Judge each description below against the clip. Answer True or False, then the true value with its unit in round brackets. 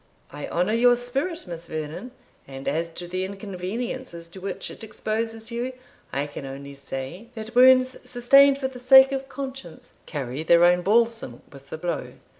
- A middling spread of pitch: False (7.3 semitones)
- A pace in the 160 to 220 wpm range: True (170 wpm)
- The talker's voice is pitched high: True (205 Hz)